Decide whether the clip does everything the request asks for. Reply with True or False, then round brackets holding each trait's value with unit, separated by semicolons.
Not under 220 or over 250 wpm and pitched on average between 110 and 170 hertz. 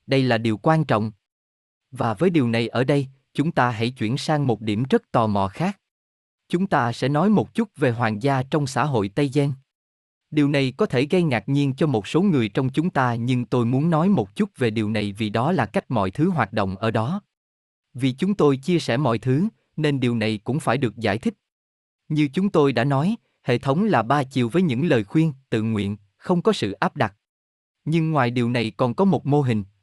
True (230 wpm; 135 Hz)